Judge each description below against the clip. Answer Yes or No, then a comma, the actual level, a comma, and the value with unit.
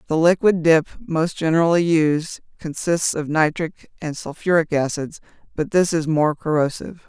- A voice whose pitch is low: No, medium, 160 Hz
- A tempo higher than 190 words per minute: No, average, 145 wpm